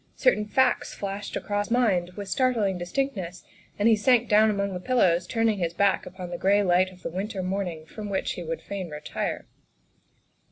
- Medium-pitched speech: No, high, 200 Hz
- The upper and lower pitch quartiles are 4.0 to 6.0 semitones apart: No, average, 3.0 semitones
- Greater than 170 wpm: Yes, average, 190 wpm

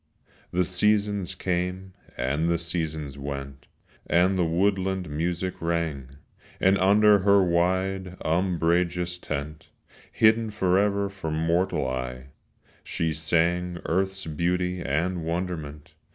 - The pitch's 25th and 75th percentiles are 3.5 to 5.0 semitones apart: No, average, 3.0 semitones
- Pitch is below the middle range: Yes, very low, 90 Hz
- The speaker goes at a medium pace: No, slow, 110 wpm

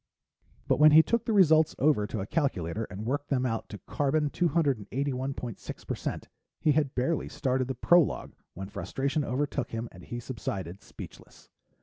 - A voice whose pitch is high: No, low, 135 Hz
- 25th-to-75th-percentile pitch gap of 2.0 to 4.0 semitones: No, average, 5.0 semitones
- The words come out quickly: No, average, 155 wpm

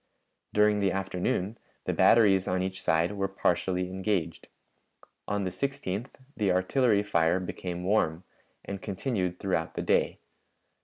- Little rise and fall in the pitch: Yes, narrow, 2.2 semitones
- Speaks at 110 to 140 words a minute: Yes, slow, 135 wpm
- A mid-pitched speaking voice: No, very low, 95 Hz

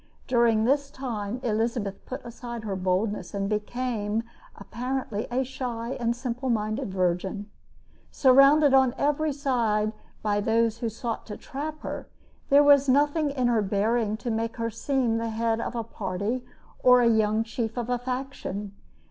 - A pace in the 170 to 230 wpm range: No, average, 155 wpm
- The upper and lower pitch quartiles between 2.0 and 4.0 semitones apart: Yes, average, 3.3 semitones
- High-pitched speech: Yes, high, 235 Hz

